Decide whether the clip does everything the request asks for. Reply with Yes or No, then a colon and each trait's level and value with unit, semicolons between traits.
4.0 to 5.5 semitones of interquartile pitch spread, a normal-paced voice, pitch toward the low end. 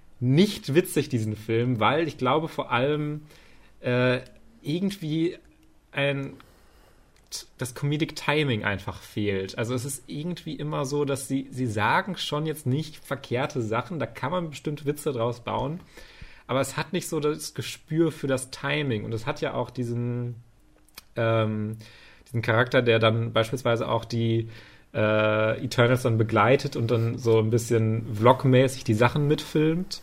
Yes: average, 4.5 semitones; average, 150 wpm; low, 130 Hz